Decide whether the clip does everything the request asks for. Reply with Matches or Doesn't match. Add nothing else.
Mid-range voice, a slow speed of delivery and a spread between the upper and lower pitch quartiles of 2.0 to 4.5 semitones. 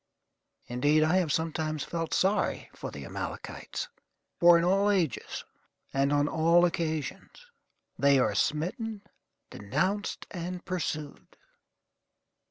Matches